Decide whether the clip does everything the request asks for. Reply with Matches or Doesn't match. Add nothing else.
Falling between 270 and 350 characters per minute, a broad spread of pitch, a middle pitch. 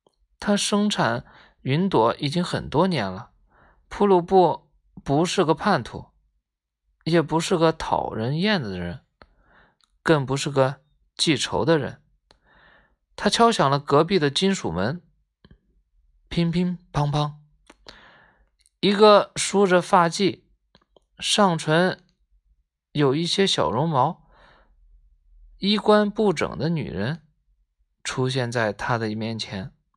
Doesn't match